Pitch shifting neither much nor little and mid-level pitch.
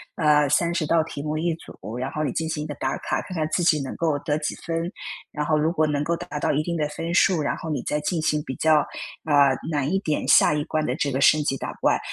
No: narrow, 1.9 semitones; medium, 155 Hz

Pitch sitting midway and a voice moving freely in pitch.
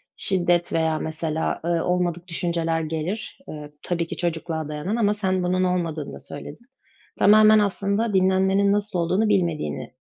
No: medium, 180 Hz; average, 3.5 semitones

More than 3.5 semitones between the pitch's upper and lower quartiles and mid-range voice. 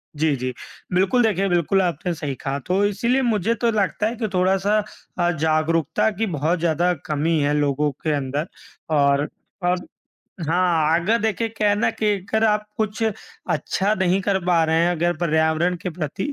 Yes: average, 4.5 semitones; medium, 175 Hz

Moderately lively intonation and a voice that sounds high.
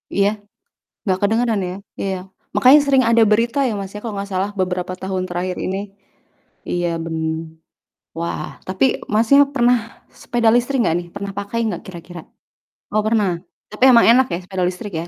Yes: average, 4.3 semitones; high, 200 Hz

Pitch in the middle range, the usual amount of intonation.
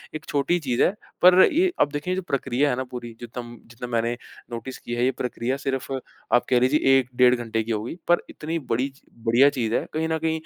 No: low, 130 Hz; average, 3.6 semitones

